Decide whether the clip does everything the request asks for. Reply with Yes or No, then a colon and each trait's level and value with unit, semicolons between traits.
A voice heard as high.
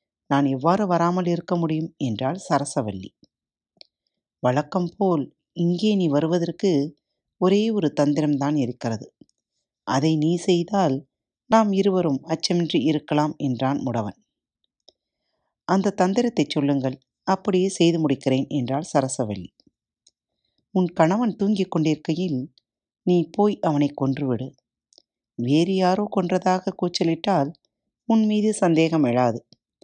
No: medium, 160 Hz